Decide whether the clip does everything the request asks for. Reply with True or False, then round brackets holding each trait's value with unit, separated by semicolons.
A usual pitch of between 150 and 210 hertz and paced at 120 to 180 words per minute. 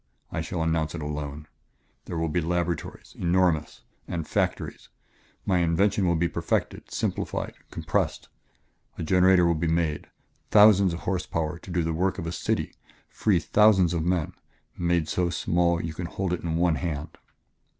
False (85 Hz; 160 wpm)